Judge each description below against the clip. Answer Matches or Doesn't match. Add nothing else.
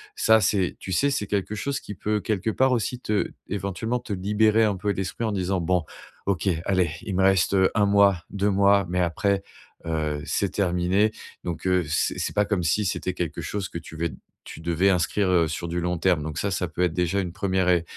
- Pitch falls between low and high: Doesn't match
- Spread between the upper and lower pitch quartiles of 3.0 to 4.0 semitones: Doesn't match